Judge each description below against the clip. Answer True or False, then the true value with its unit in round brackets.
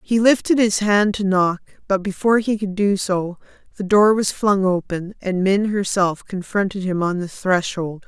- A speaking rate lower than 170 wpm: False (185 wpm)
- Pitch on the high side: True (195 Hz)